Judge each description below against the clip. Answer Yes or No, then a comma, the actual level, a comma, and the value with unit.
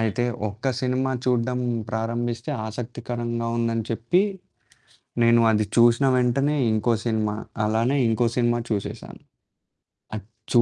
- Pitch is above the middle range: No, low, 115 Hz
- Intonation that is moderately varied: No, narrow, 1.6 semitones